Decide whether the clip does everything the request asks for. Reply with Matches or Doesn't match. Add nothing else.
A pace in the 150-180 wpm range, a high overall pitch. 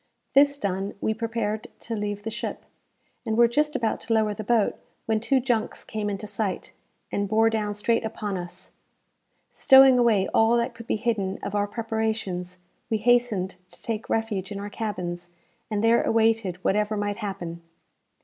Matches